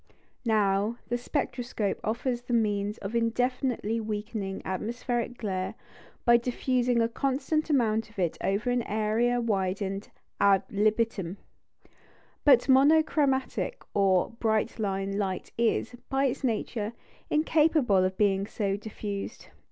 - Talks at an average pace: No, slow, 120 wpm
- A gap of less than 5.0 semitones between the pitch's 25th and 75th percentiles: Yes, average, 3.6 semitones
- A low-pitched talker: No, high, 225 Hz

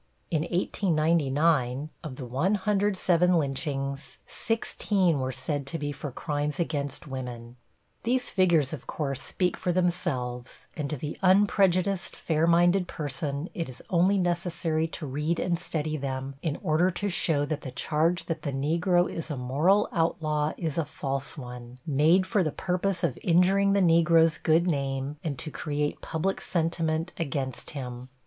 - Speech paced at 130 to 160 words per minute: Yes, average, 155 wpm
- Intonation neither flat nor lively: Yes, average, 4.0 semitones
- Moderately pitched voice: Yes, medium, 160 Hz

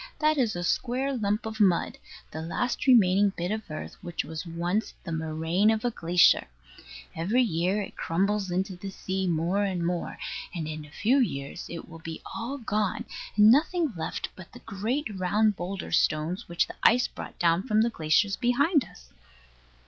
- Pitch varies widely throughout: No, average, 4.8 semitones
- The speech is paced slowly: No, average, 180 wpm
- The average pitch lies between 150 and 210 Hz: Yes, high, 190 Hz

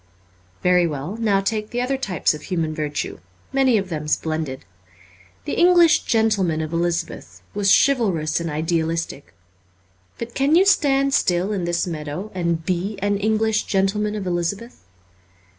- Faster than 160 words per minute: No, average, 145 wpm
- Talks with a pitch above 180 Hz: Yes, high, 190 Hz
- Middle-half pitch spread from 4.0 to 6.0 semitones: Yes, average, 5.0 semitones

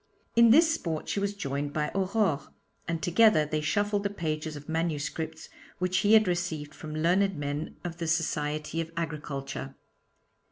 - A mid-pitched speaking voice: Yes, medium, 165 Hz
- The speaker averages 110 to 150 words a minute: No, average, 160 wpm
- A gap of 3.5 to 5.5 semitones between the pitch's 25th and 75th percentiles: Yes, average, 4.2 semitones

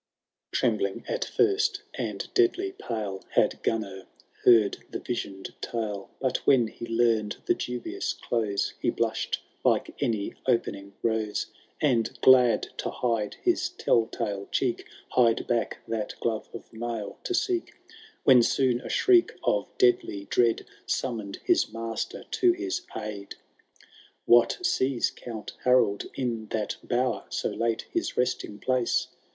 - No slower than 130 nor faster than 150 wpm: Yes, average, 140 wpm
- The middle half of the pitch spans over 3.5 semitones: No, average, 3.2 semitones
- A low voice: Yes, low, 115 Hz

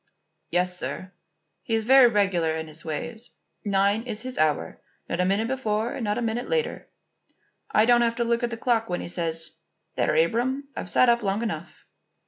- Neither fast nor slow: Yes, average, 195 wpm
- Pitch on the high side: Yes, high, 220 Hz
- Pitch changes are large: No, average, 5.0 semitones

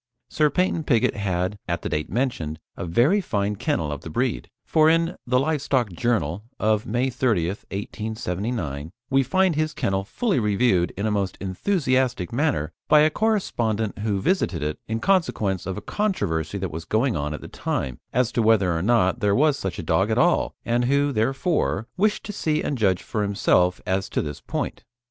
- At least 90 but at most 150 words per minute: No, average, 190 wpm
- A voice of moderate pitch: No, low, 110 Hz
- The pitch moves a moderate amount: No, wide, 6.8 semitones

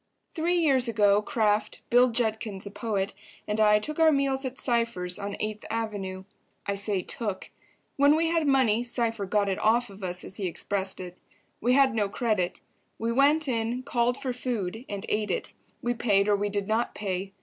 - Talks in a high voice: Yes, high, 220 Hz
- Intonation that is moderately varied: Yes, average, 3.7 semitones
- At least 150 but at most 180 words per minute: No, average, 190 wpm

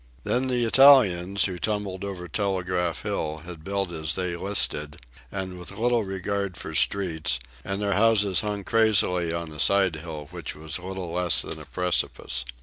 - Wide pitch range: No, average, 2.8 semitones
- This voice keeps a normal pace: Yes, average, 165 wpm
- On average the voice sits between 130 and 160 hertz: No, very low, 95 Hz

